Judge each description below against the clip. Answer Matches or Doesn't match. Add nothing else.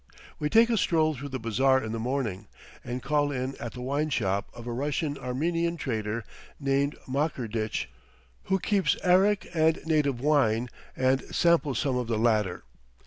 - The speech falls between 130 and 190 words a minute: Matches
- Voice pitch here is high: Doesn't match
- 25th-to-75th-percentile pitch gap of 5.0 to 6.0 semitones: Doesn't match